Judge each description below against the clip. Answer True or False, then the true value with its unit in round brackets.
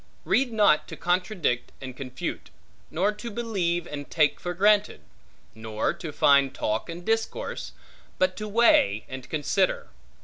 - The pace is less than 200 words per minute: True (140 wpm)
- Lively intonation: True (7.4 semitones)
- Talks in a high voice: False (175 Hz)